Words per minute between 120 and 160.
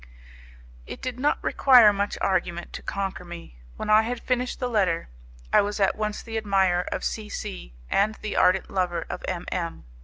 No: average, 185 wpm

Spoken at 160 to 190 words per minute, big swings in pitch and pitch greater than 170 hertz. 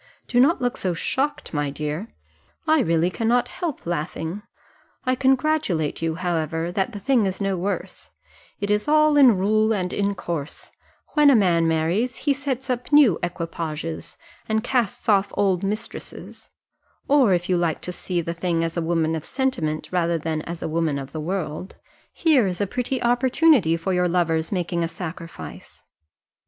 Yes: average, 170 wpm; wide, 6.7 semitones; medium, 185 Hz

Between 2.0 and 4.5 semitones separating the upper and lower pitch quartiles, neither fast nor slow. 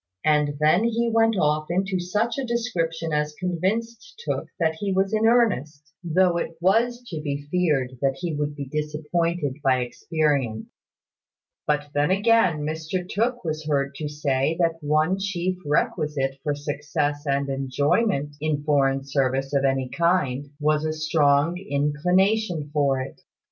Yes: average, 4.1 semitones; average, 150 wpm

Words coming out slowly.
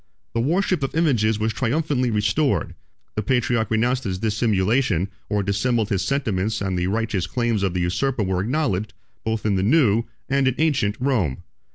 No: average, 170 wpm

